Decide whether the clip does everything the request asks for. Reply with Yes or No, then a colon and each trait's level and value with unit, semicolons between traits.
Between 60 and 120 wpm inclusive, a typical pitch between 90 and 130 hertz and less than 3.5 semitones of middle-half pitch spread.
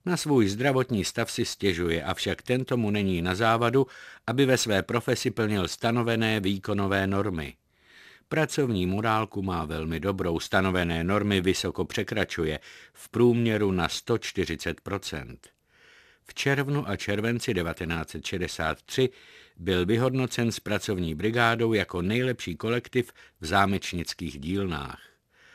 No: slow, 115 wpm; low, 100 Hz; average, 4.6 semitones